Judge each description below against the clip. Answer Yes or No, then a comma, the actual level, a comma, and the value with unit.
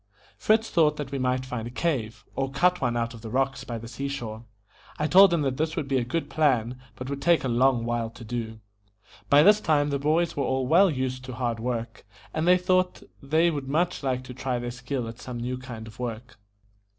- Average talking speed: No, fast, 235 wpm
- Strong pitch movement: No, average, 4.0 semitones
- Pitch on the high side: No, low, 130 Hz